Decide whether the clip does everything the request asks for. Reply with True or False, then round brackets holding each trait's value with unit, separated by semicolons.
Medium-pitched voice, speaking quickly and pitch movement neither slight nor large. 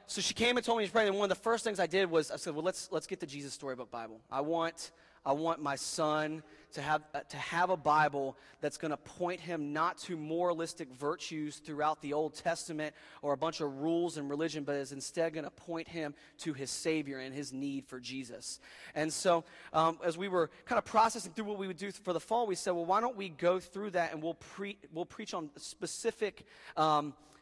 True (160 Hz; 240 wpm; 3.4 semitones)